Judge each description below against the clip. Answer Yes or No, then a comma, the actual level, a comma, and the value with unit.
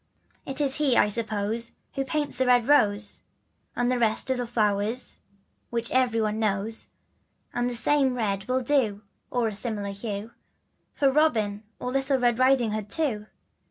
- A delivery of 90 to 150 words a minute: No, average, 165 wpm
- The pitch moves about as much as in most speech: Yes, average, 3.4 semitones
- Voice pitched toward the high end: Yes, high, 235 Hz